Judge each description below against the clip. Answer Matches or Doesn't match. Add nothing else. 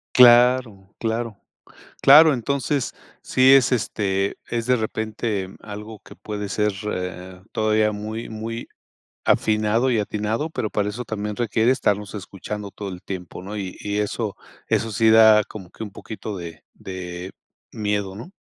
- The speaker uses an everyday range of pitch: Doesn't match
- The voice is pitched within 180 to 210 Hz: Doesn't match